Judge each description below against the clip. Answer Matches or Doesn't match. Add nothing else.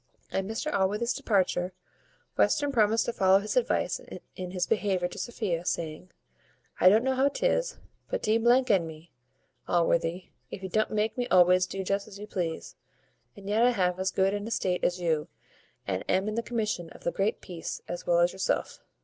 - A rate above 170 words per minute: Matches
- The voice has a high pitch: Matches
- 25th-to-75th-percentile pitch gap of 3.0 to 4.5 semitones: Matches